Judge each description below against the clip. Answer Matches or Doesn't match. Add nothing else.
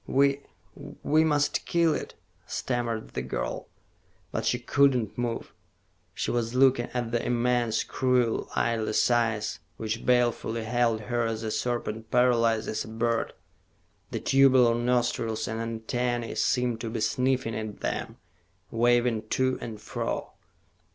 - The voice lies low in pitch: Matches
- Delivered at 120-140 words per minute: Matches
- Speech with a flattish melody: Matches